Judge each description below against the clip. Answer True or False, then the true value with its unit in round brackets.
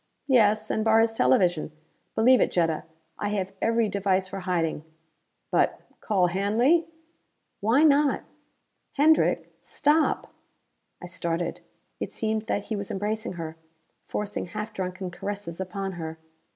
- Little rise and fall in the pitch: False (3.7 semitones)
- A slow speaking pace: True (130 wpm)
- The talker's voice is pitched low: False (200 Hz)